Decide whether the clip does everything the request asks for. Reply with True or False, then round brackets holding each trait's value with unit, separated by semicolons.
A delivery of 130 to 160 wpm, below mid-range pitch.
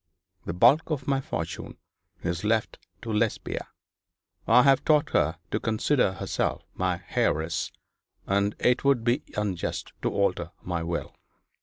True (140 wpm; 105 Hz)